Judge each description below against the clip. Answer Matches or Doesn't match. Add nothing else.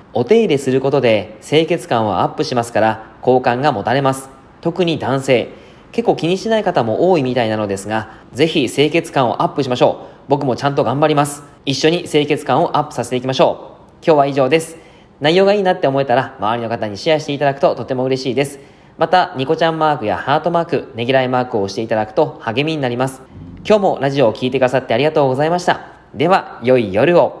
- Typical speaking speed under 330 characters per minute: Doesn't match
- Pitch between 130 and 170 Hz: Matches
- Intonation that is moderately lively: Matches